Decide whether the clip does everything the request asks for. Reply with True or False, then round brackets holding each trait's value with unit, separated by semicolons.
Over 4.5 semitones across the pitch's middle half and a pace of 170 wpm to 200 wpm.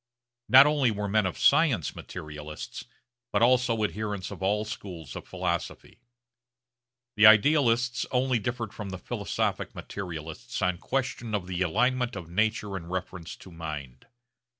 False (5.1 semitones; 140 wpm)